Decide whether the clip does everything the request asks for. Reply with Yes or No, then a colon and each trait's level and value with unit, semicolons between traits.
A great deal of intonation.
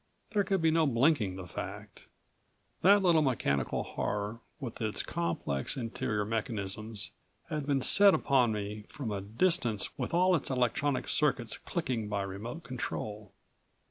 Yes: wide, 6.3 semitones